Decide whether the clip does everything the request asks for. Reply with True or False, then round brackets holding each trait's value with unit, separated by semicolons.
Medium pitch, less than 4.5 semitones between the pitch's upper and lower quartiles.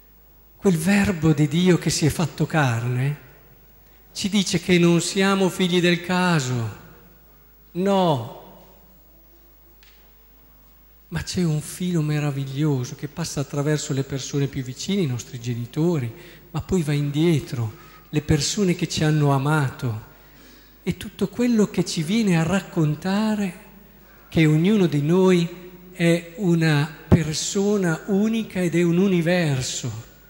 True (170 Hz; 3.7 semitones)